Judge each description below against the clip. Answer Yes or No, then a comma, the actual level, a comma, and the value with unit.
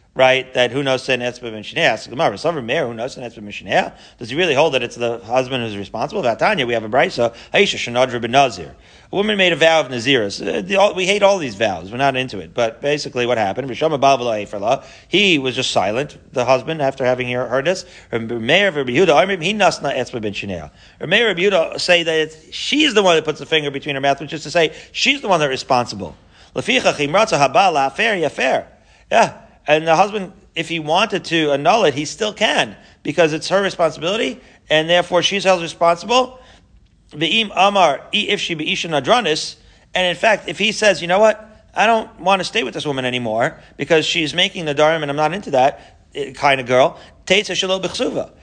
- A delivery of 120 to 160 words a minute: No, average, 175 wpm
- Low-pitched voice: No, medium, 155 Hz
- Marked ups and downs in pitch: Yes, wide, 6.7 semitones